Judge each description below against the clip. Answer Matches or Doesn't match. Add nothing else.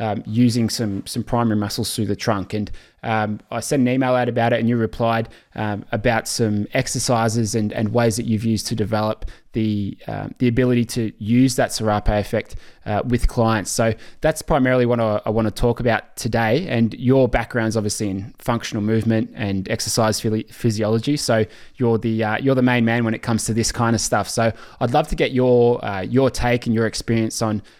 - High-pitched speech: Doesn't match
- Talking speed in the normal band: Doesn't match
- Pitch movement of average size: Doesn't match